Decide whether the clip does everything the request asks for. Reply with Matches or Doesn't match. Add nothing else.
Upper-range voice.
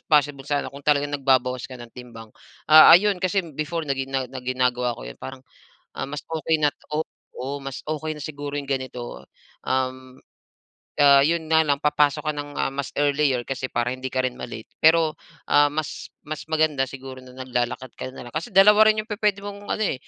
Doesn't match